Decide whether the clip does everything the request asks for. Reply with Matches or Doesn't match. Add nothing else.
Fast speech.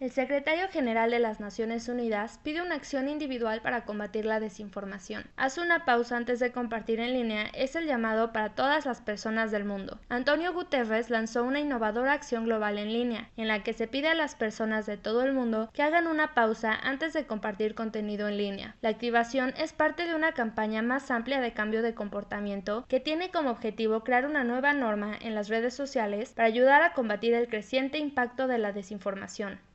Matches